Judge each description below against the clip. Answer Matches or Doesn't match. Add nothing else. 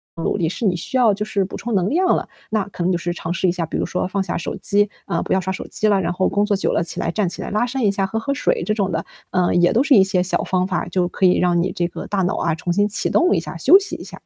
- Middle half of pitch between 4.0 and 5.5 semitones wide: Doesn't match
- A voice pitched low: Doesn't match